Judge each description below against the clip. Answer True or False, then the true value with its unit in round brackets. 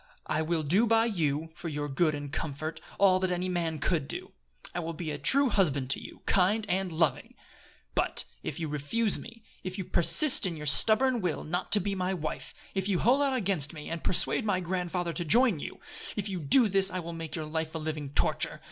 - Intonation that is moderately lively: True (4.1 semitones)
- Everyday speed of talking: False (220 wpm)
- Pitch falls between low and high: True (175 Hz)